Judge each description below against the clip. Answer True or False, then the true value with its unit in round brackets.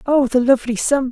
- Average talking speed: False (215 wpm)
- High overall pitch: True (260 Hz)